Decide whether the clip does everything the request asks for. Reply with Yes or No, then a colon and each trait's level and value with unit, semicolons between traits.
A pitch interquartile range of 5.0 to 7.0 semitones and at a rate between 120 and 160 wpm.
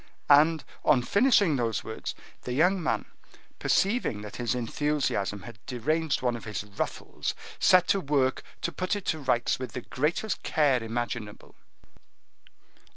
Yes: wide, 5.5 semitones; average, 145 wpm